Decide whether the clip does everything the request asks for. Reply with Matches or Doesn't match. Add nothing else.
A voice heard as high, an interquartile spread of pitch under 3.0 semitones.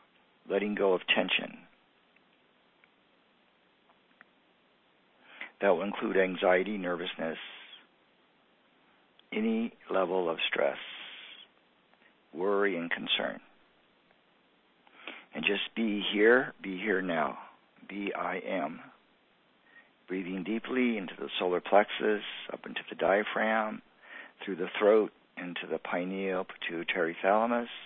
Doesn't match